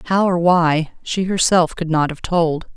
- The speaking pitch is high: No, medium, 170 Hz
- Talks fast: No, average, 195 wpm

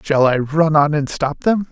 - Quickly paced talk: Yes, fast, 245 wpm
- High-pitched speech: No, medium, 150 Hz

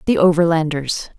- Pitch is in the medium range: Yes, medium, 165 Hz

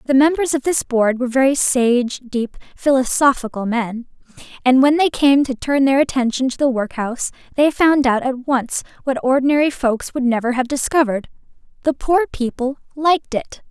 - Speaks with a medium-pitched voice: No, very high, 265 Hz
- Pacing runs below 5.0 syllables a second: No, 5.1 syllables/s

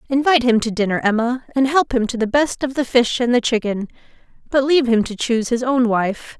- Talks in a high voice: Yes, high, 245 Hz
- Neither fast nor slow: No, fast, 235 wpm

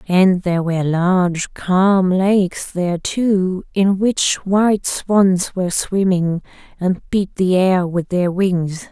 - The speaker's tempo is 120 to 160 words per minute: Yes, average, 140 wpm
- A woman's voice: Yes, female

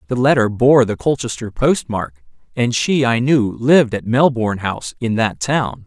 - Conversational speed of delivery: Yes, average, 185 wpm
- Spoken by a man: Yes, male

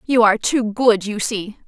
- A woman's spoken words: Yes, female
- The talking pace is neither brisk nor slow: No, fast, 215 wpm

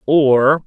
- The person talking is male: Yes, male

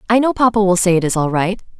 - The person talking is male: No, female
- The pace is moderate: No, fast, 300 wpm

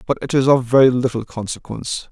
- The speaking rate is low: No, average, 200 wpm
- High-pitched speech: No, low, 125 Hz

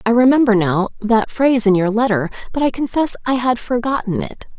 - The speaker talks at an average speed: Yes, average, 195 wpm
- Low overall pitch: No, high, 230 Hz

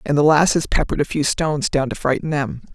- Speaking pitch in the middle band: Yes, medium, 145 Hz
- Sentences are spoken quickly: Yes, fast, 240 wpm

